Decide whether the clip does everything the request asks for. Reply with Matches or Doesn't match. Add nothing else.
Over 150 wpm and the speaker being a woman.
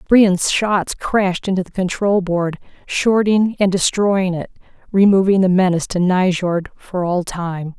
Doesn't match